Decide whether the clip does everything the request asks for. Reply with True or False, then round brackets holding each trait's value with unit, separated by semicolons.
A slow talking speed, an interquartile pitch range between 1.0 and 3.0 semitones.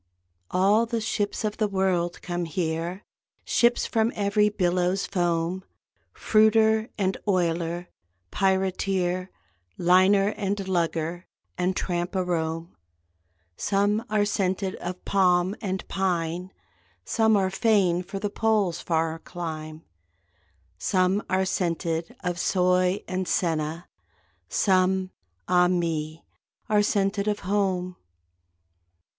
True (110 wpm; 2.5 semitones)